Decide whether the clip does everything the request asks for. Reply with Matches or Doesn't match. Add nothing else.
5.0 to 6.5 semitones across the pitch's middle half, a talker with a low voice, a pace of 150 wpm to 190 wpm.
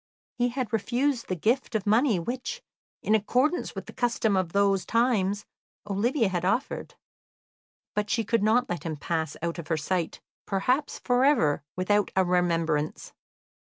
Doesn't match